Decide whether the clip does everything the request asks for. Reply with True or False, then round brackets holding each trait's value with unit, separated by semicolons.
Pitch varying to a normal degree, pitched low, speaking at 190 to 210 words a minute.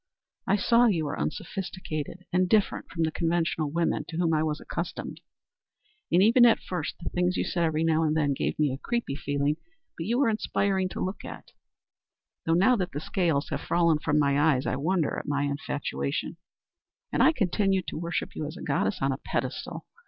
False (3.9 semitones; 165 Hz; 200 wpm)